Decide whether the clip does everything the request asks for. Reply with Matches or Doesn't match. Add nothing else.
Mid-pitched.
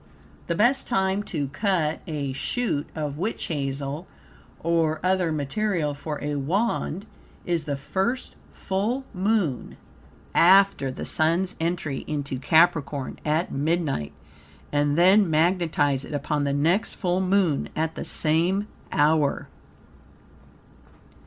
Matches